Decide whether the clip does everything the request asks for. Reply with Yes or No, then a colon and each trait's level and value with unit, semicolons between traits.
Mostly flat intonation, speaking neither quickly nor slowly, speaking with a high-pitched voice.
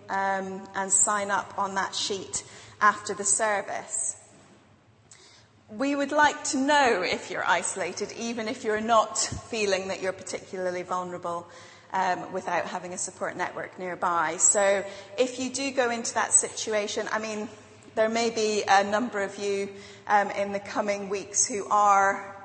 Yes: narrow, 2.2 semitones; average, 155 wpm; high, 200 Hz